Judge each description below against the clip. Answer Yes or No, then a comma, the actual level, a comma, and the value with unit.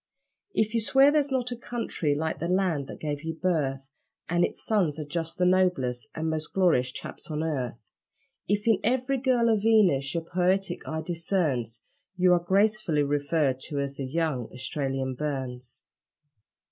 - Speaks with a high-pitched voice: No, medium, 160 Hz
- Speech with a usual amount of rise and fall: No, wide, 5.7 semitones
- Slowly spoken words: No, average, 170 wpm